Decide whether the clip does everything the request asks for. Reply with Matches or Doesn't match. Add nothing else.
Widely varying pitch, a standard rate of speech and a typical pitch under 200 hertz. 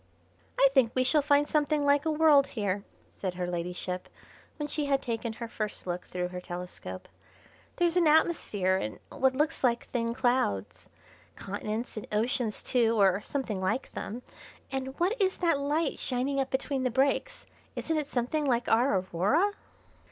Doesn't match